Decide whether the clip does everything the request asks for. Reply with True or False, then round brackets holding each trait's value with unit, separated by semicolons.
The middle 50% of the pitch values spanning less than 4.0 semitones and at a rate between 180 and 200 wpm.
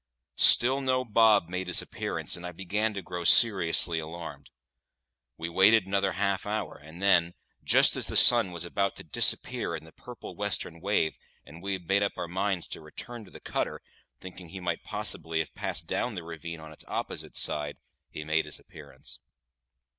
True (3.5 semitones; 185 wpm)